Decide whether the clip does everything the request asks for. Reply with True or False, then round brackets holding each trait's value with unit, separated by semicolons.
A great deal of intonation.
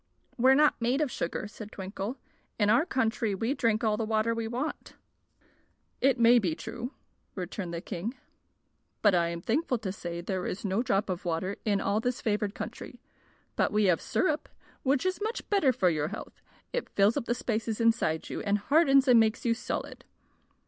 False (4.1 semitones)